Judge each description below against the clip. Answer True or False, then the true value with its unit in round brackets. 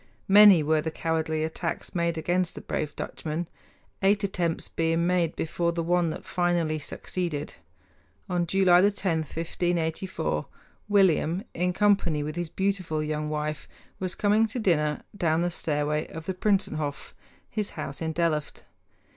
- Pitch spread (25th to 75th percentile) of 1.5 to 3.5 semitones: True (2.8 semitones)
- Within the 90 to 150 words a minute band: True (145 wpm)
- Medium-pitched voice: True (170 Hz)